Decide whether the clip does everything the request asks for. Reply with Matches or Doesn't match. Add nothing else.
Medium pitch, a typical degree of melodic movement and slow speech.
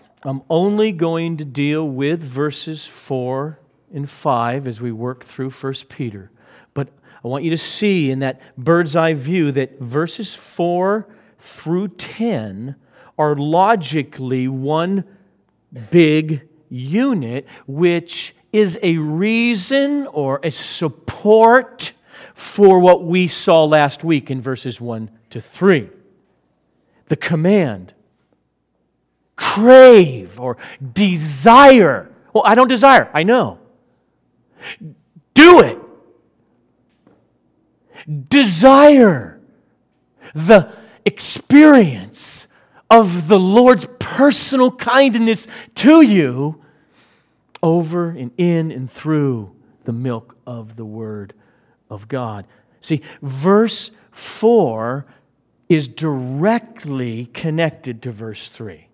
Doesn't match